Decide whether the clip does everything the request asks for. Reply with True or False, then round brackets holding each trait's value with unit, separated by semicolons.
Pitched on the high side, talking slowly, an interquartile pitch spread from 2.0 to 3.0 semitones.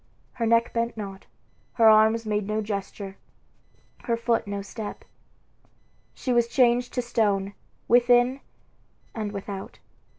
True (225 Hz; 125 wpm; 2.7 semitones)